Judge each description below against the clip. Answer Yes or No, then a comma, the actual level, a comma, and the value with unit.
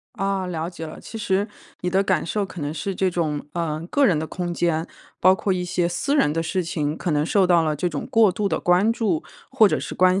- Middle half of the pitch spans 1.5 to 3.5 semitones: Yes, average, 3.2 semitones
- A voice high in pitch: No, medium, 180 Hz